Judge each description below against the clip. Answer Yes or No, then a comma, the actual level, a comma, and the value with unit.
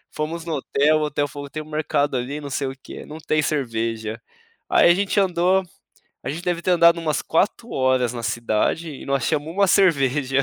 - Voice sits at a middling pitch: Yes, medium, 150 Hz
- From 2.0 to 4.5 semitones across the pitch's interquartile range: Yes, average, 4.2 semitones